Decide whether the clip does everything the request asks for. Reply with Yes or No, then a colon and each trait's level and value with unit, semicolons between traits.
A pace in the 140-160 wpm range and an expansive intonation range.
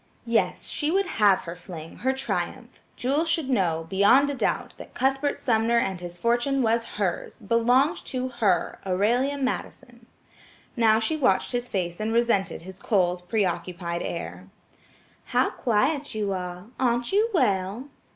Yes: average, 145 wpm; wide, 5.9 semitones